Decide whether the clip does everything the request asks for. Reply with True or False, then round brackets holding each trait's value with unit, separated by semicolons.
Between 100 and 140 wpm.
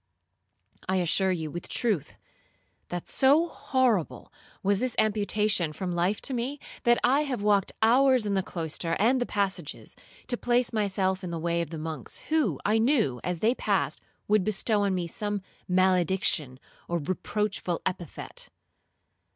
False (155 wpm)